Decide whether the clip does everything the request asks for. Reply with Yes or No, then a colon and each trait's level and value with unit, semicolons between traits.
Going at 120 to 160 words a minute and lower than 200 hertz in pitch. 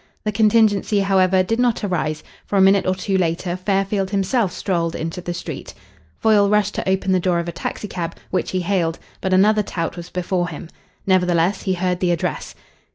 No: average, 190 wpm; medium, 185 Hz